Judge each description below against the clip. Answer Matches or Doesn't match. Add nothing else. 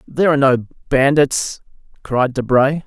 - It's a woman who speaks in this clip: Doesn't match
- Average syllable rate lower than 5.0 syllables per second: Matches